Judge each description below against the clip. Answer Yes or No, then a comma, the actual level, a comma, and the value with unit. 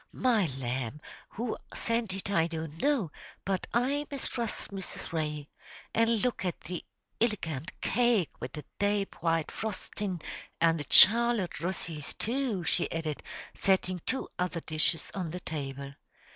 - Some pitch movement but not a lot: No, wide, 6.0 semitones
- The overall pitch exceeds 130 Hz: Yes, medium, 185 Hz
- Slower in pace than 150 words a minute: Yes, average, 140 wpm